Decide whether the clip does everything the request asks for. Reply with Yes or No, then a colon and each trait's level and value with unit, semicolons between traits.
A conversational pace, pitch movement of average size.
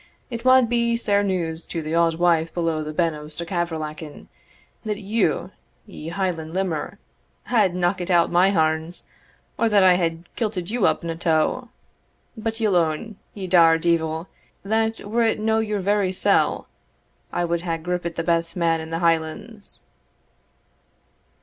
Yes: average, 160 wpm; average, 3.9 semitones